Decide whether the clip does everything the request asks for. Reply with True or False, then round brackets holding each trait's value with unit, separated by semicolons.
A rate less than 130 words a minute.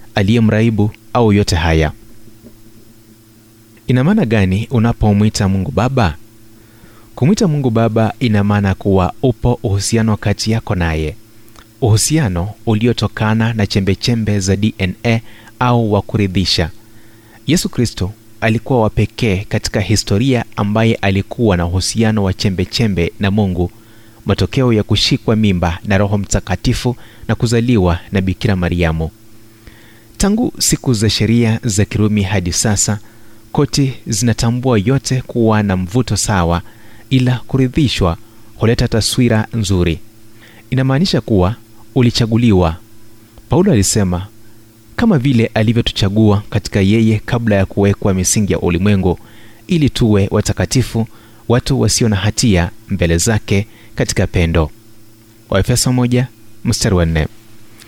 True (105 wpm)